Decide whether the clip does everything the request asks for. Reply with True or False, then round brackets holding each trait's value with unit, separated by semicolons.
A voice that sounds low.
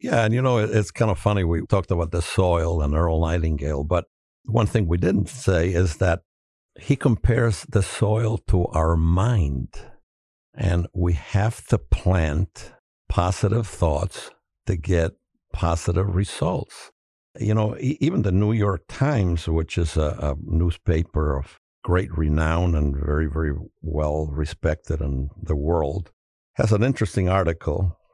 True (85 Hz)